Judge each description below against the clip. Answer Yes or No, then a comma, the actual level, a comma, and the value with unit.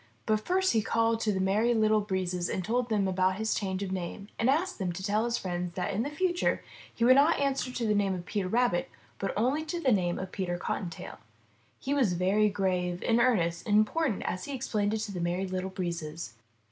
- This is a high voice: Yes, high, 205 Hz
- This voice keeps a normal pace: No, fast, 230 wpm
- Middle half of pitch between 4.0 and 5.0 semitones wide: Yes, average, 4.3 semitones